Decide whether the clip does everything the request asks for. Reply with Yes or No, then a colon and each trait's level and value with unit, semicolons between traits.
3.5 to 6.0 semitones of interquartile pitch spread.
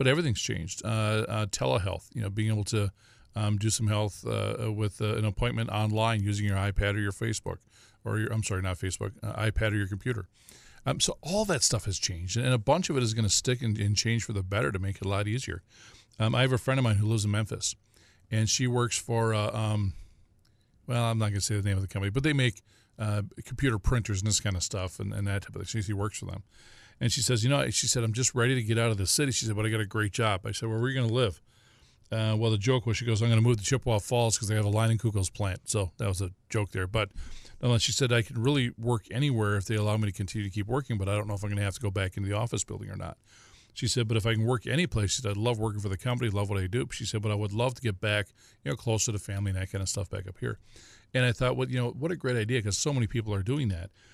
No: average, 2.7 semitones